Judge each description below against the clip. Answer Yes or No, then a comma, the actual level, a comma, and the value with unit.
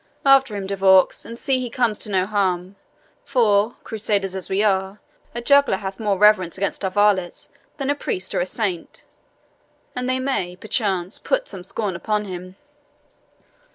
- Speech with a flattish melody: No, average, 3.5 semitones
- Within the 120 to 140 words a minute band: No, average, 170 wpm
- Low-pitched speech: No, high, 205 Hz